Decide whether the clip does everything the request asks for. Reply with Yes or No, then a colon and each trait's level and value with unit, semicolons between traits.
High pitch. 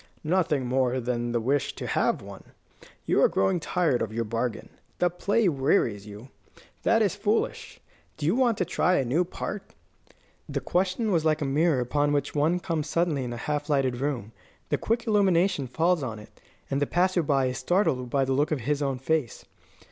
No: medium, 145 Hz